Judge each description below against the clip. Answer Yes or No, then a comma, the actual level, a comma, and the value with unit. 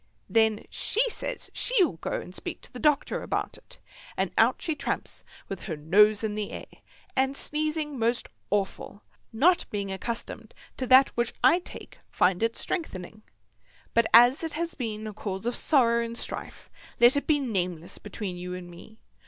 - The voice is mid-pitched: No, high, 230 Hz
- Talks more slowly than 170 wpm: No, average, 175 wpm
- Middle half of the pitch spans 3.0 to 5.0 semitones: No, wide, 5.6 semitones